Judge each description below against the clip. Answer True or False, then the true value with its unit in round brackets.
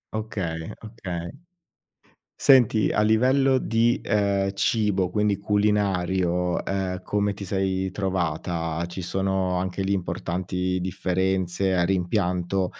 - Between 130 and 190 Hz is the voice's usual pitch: False (95 Hz)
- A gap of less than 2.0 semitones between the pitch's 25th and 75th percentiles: False (2.3 semitones)